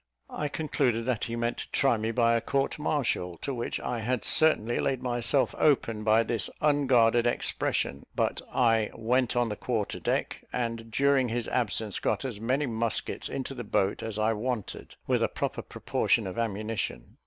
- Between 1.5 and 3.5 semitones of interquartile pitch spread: Yes, narrow, 2.6 semitones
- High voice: No, low, 120 Hz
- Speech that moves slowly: No, average, 175 wpm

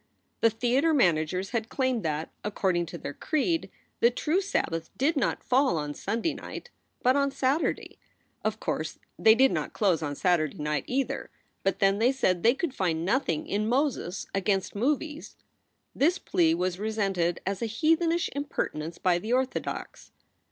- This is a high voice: Yes, high, 220 Hz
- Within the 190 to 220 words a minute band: No, average, 160 wpm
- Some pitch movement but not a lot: No, wide, 7.6 semitones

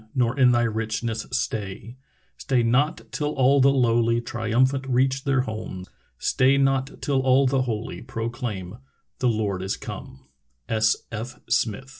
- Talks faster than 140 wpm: No, slow, 135 wpm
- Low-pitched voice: Yes, low, 120 Hz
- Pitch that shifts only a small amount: No, average, 3.1 semitones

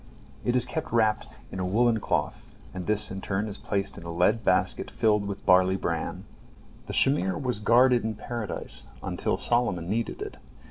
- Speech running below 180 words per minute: No, average, 185 wpm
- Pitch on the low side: Yes, low, 105 Hz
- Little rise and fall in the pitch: No, average, 3.8 semitones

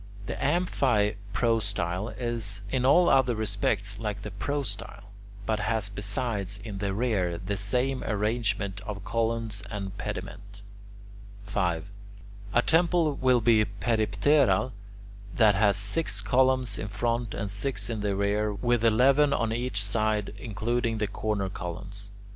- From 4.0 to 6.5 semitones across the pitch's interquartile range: No, average, 3.1 semitones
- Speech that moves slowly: Yes, slow, 130 wpm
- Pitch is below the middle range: Yes, low, 105 Hz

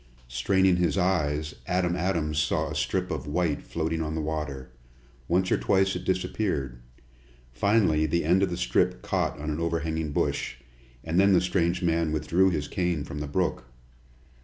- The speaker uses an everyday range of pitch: Yes, average, 3.0 semitones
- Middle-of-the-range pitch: No, very low, 85 Hz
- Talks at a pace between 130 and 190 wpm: Yes, average, 170 wpm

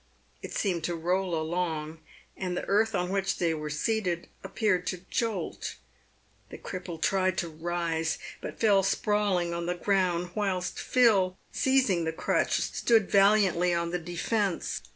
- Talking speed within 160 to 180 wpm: No, average, 150 wpm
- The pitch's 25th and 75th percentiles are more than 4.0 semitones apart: No, average, 2.7 semitones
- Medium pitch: Yes, medium, 180 Hz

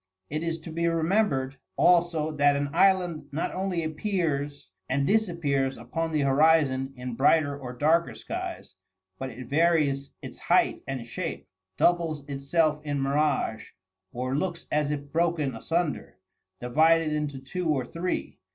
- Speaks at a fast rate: No, average, 140 wpm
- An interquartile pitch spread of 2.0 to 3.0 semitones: No, average, 3.4 semitones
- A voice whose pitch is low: No, medium, 150 Hz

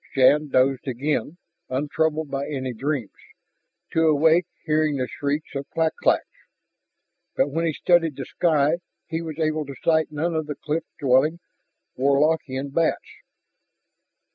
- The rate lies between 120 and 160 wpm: Yes, average, 140 wpm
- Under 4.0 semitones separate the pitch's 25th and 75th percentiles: Yes, narrow, 2.5 semitones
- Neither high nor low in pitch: Yes, medium, 150 Hz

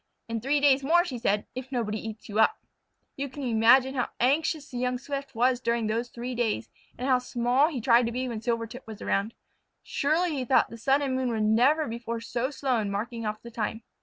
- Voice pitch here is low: No, high, 245 Hz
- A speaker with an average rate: No, fast, 220 wpm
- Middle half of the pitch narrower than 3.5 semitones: Yes, average, 2.8 semitones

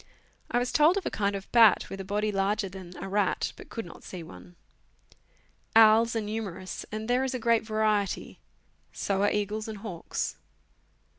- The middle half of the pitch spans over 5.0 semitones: No, narrow, 2.6 semitones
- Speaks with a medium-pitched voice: No, high, 210 Hz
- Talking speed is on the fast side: No, average, 180 wpm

